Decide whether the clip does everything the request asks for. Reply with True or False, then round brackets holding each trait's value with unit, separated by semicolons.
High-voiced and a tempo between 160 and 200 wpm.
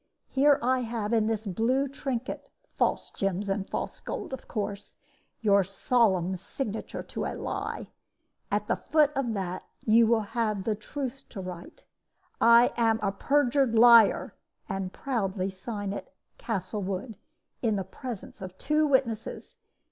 False (220 Hz; 145 wpm)